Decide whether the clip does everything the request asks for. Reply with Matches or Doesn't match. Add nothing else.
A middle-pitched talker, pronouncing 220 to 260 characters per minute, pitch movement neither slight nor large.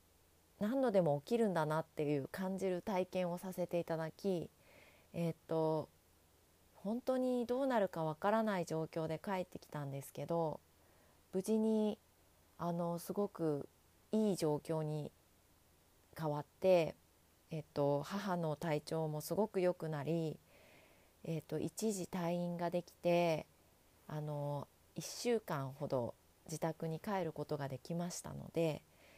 Matches